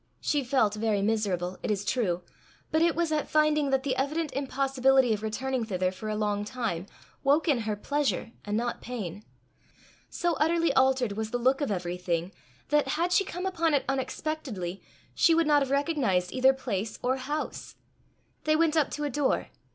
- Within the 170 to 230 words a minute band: Yes, average, 180 wpm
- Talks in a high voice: Yes, very high, 260 Hz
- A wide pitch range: Yes, wide, 5.9 semitones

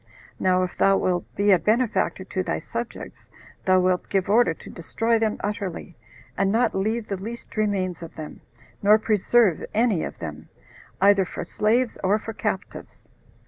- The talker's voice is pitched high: Yes, high, 200 Hz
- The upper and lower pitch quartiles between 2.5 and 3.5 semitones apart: Yes, average, 3.1 semitones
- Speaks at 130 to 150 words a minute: No, average, 165 wpm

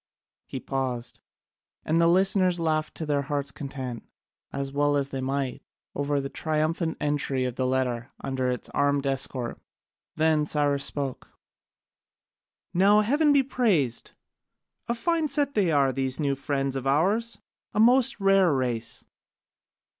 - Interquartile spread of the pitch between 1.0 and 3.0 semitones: No, average, 5.2 semitones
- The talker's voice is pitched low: No, medium, 145 Hz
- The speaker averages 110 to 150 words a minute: Yes, average, 140 wpm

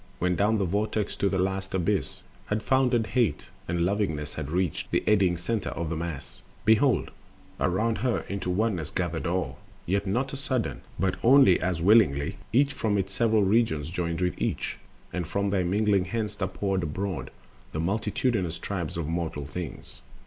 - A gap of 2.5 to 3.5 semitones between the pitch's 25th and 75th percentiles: No, average, 4.0 semitones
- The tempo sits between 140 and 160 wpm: No, average, 170 wpm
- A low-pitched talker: Yes, very low, 95 Hz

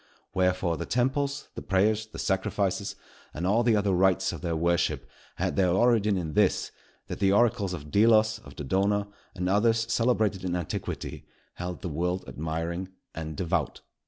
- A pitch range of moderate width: Yes, average, 3.8 semitones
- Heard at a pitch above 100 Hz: No, very low, 95 Hz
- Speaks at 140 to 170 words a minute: Yes, average, 160 wpm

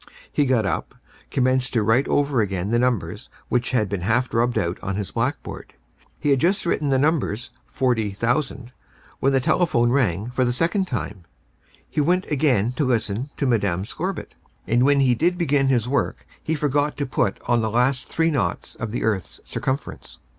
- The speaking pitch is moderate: No, low, 125 Hz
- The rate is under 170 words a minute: No, average, 180 wpm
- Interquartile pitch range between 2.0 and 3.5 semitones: No, average, 4.2 semitones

